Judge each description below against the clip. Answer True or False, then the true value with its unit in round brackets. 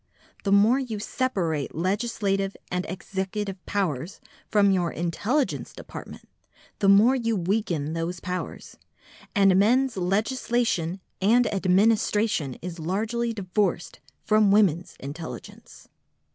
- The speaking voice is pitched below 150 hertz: False (195 Hz)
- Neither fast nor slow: False (110 wpm)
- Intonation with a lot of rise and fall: False (3.6 semitones)